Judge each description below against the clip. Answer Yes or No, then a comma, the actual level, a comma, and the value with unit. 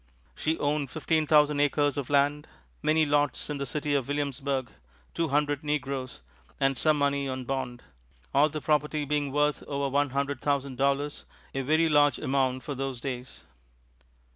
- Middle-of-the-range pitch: Yes, medium, 145 Hz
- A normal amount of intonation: No, narrow, 1.5 semitones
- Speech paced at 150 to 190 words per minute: Yes, average, 165 wpm